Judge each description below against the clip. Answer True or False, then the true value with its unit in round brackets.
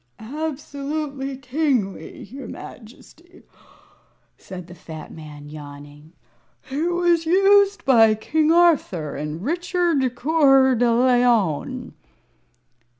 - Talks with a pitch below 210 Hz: False (265 Hz)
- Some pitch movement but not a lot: False (8.7 semitones)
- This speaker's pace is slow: True (90 wpm)